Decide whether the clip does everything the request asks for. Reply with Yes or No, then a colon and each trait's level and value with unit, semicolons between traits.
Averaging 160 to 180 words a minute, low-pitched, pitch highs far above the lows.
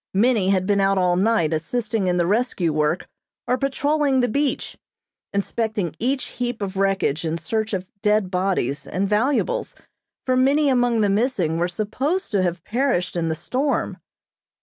No: average, 165 wpm; high, 210 Hz; wide, 5.7 semitones